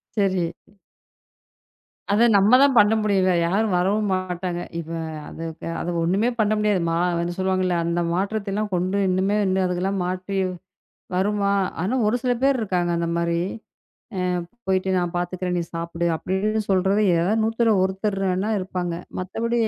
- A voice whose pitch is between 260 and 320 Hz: No, high, 190 Hz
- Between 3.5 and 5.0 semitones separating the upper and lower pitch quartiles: No, narrow, 2.6 semitones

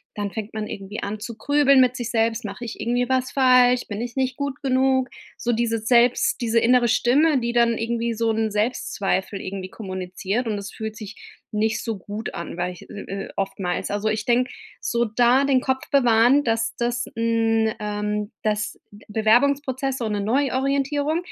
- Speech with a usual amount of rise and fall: Yes, average, 3.1 semitones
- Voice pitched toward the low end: No, high, 230 Hz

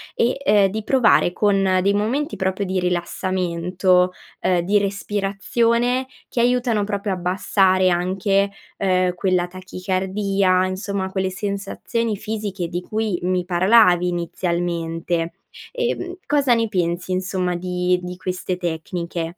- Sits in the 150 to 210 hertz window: Yes, medium, 185 Hz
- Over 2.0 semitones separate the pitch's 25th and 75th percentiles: Yes, narrow, 2.4 semitones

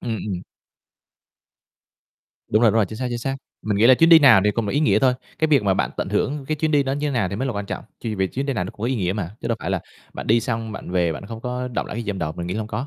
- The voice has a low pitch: Yes, low, 115 Hz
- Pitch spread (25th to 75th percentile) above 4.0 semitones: Yes, average, 5.0 semitones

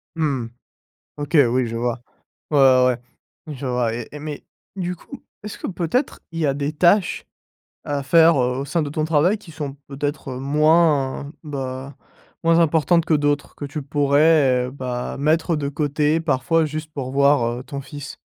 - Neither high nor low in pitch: Yes, medium, 145 Hz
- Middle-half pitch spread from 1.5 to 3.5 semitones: Yes, average, 3.0 semitones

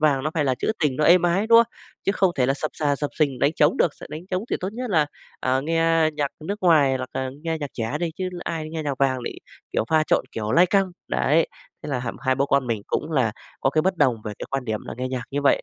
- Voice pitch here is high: No, medium, 150 Hz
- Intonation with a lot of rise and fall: No, average, 4.0 semitones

